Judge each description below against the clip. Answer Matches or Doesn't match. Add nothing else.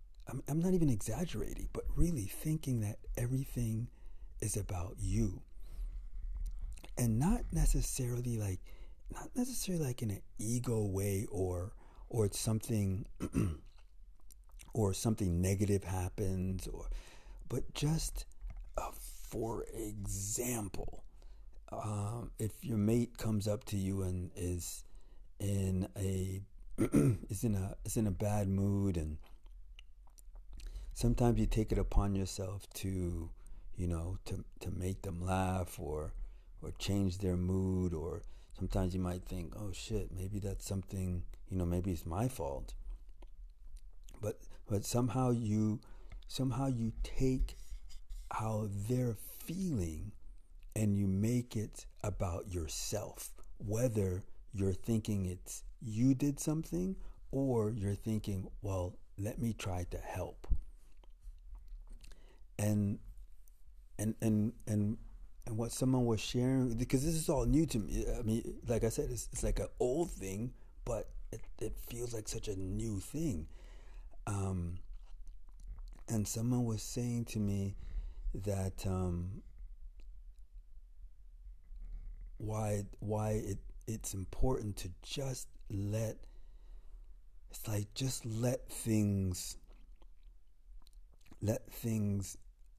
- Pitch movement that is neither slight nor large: Matches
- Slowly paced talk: Matches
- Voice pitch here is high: Doesn't match